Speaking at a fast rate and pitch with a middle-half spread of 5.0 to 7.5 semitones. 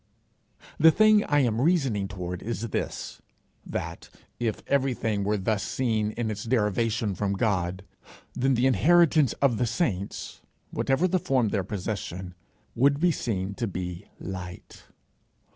No: average, 145 wpm; average, 5.3 semitones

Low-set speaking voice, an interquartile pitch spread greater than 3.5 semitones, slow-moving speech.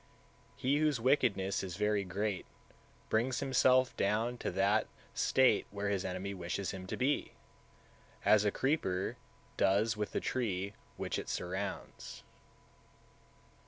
Yes: low, 105 Hz; average, 4.4 semitones; slow, 130 wpm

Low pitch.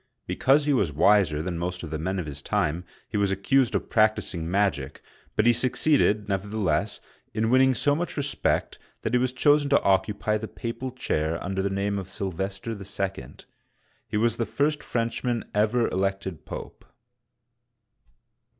Yes: low, 105 Hz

